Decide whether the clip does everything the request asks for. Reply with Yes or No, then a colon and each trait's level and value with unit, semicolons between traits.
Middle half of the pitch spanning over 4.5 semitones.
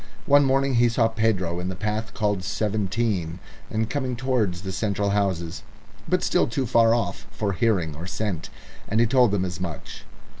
No: average, 3.9 semitones